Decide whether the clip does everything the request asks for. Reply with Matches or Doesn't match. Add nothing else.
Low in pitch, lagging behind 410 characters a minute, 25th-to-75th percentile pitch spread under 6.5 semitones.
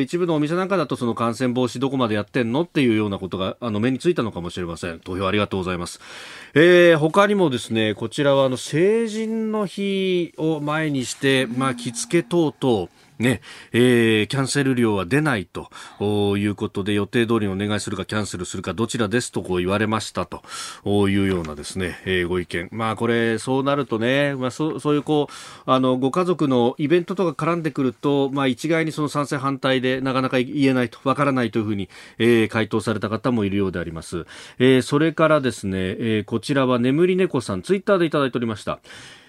Doesn't match